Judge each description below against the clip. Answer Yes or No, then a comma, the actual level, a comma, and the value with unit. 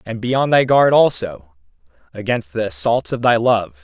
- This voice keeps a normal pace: Yes, average, 190 wpm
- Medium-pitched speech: No, low, 110 Hz